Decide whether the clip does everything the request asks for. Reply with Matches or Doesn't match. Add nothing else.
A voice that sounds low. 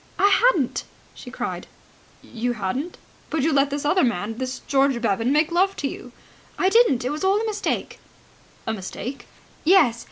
Doesn't match